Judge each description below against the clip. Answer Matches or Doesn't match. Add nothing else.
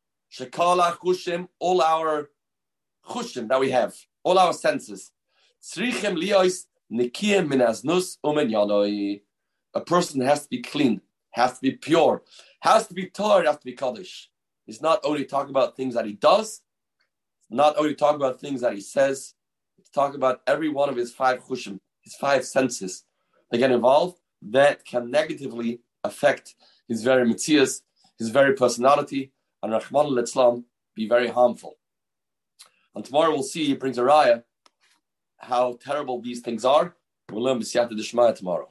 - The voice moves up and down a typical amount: Matches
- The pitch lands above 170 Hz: Doesn't match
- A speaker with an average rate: Matches